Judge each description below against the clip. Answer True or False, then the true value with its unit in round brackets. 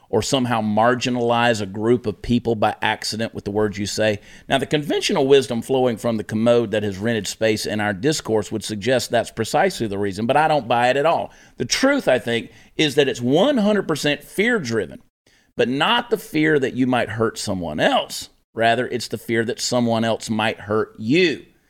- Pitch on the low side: True (115 Hz)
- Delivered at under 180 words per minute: False (200 wpm)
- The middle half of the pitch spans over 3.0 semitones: True (4.1 semitones)